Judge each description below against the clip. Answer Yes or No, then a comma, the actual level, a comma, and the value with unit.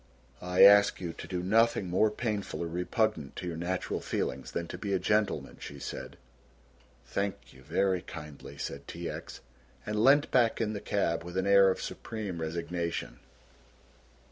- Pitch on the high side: No, very low, 95 Hz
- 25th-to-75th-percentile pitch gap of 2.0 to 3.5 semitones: No, average, 3.9 semitones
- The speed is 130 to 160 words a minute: No, average, 170 wpm